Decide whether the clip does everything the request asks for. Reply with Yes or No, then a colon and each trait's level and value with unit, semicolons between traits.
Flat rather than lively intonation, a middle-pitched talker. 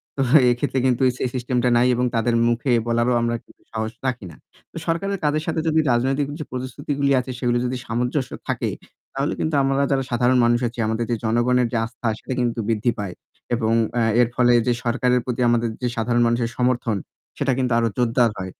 No: narrow, 1.8 semitones; low, 125 Hz